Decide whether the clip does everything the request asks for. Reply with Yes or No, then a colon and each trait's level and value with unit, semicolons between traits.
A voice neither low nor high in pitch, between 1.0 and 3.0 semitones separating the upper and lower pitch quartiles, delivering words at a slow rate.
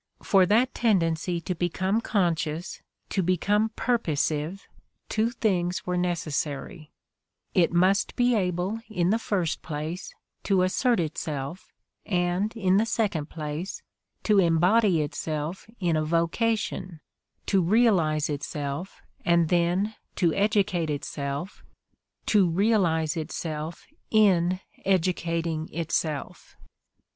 No: medium, 175 Hz; average, 3.7 semitones; slow, 110 wpm